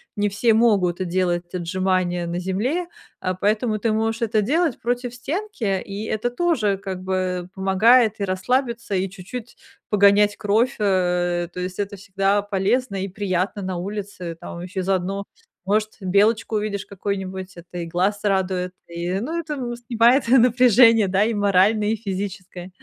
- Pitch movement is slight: No, average, 3.4 semitones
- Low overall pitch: No, high, 200 Hz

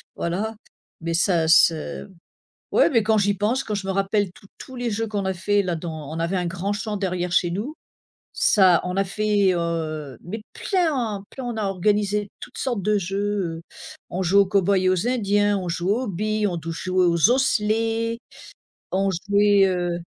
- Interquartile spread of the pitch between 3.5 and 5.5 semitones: No, average, 3.1 semitones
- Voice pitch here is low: No, high, 195 Hz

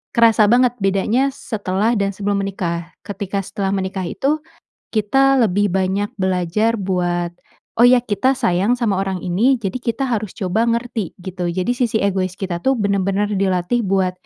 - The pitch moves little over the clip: No, average, 3.6 semitones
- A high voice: Yes, high, 200 Hz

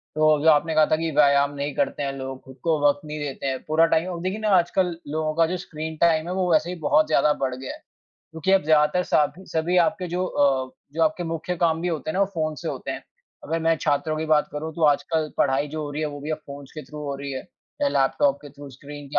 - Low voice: No, medium, 155 Hz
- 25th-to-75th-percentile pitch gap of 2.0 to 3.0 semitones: Yes, narrow, 2.4 semitones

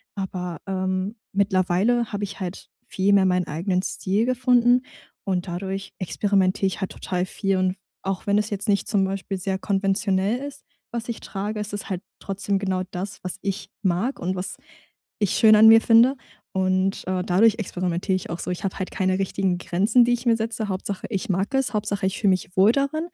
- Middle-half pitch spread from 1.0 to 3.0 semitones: Yes, narrow, 2.4 semitones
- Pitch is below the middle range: No, high, 195 Hz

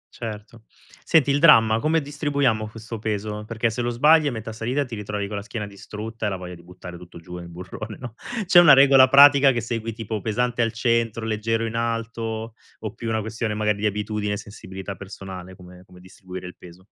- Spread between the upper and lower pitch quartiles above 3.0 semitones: No, average, 2.7 semitones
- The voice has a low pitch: Yes, low, 110 Hz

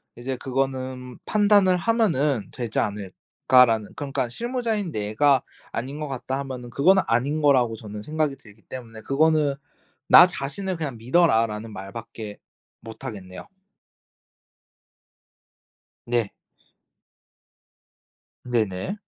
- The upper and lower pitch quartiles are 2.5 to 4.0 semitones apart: No, average, 5.2 semitones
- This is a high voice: No, low, 130 Hz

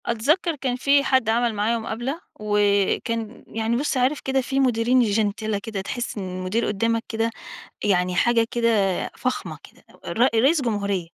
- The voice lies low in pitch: No, high, 230 Hz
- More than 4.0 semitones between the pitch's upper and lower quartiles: No, average, 3.4 semitones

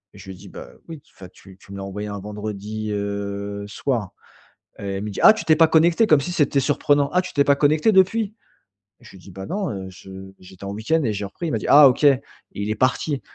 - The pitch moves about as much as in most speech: No, wide, 7.1 semitones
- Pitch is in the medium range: No, low, 110 Hz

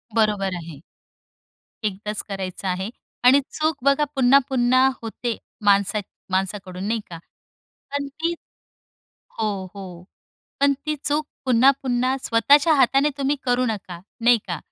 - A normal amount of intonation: No, wide, 5.7 semitones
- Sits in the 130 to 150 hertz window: No, high, 240 Hz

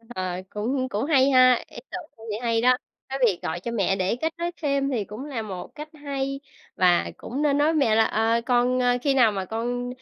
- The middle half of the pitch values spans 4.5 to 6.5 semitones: No, average, 4.0 semitones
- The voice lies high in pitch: Yes, high, 245 Hz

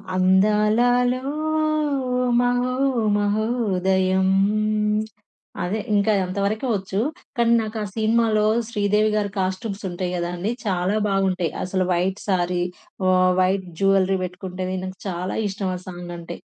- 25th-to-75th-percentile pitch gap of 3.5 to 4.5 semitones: No, narrow, 2.5 semitones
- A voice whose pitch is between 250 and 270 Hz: No, high, 195 Hz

